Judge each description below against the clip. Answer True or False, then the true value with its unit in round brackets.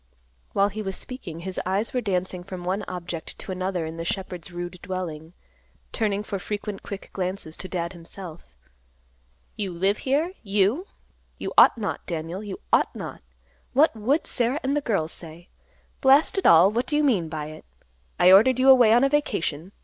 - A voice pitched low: False (195 Hz)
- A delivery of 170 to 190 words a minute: True (180 wpm)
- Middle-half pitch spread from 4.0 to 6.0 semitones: True (4.8 semitones)